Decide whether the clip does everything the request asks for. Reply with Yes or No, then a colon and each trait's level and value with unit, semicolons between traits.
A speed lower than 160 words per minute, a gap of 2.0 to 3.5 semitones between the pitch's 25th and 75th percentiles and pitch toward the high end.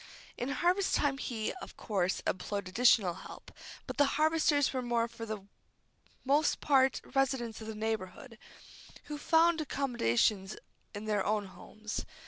No: slow, 135 wpm; average, 5.0 semitones; high, 235 Hz